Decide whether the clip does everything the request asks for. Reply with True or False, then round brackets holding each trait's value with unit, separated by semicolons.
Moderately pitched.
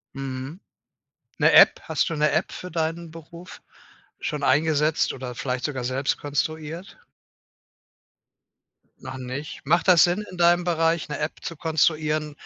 True (155 Hz)